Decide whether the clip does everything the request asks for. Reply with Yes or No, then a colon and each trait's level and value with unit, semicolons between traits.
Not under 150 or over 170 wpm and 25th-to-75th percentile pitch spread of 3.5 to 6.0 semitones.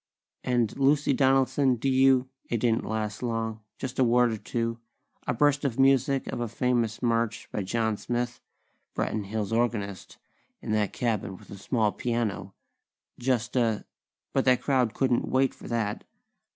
No: average, 160 wpm; average, 2.9 semitones